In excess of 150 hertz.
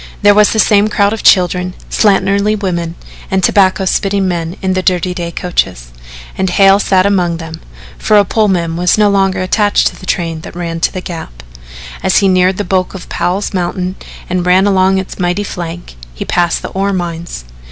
Yes: medium, 185 Hz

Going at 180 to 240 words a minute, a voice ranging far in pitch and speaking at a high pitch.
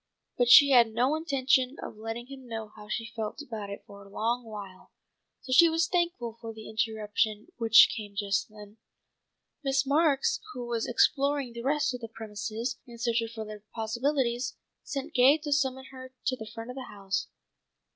No: average, 185 wpm; average, 3.6 semitones; high, 235 Hz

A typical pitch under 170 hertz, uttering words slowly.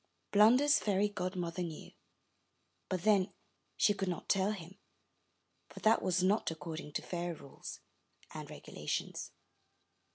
No: medium, 185 Hz; slow, 125 wpm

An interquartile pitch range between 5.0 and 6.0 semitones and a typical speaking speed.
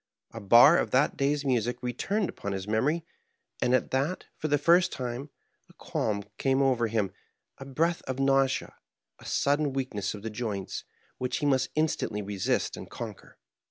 No: average, 4.2 semitones; average, 170 wpm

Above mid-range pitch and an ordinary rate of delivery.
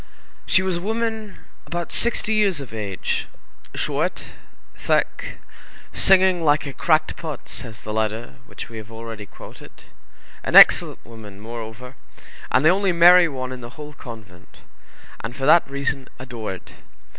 No: low, 135 Hz; average, 145 wpm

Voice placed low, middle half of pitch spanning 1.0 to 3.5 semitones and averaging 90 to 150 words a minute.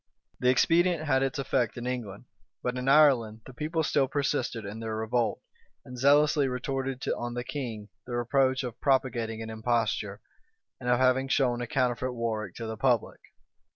No: low, 125 Hz; average, 2.7 semitones; average, 170 wpm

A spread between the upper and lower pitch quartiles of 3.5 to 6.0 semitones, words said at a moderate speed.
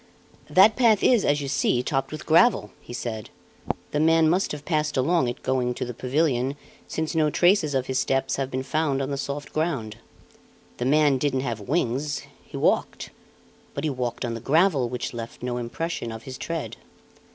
Yes: average, 4.2 semitones; average, 190 wpm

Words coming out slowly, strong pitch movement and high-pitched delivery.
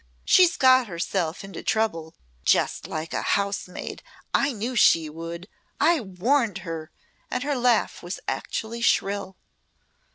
Yes: slow, 130 wpm; wide, 6.5 semitones; high, 200 Hz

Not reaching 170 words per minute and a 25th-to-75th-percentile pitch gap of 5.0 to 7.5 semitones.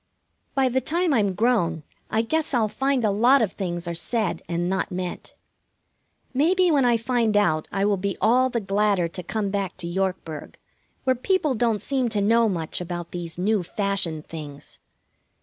No: average, 180 wpm; wide, 5.5 semitones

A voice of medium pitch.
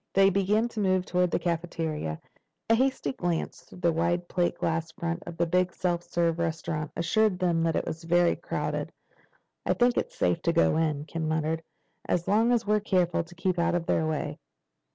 Yes: medium, 170 Hz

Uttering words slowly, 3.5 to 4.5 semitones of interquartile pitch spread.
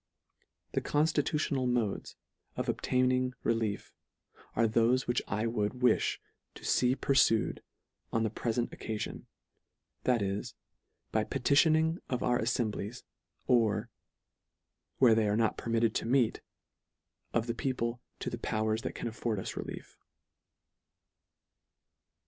No: slow, 125 wpm; narrow, 2.5 semitones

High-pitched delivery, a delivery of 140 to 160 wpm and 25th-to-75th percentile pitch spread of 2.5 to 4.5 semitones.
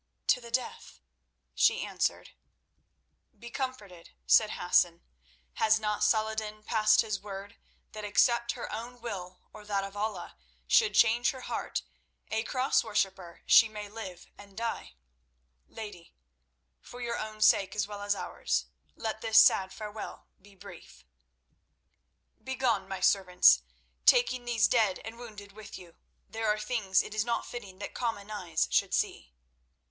Yes: high, 215 Hz; average, 150 wpm; average, 2.8 semitones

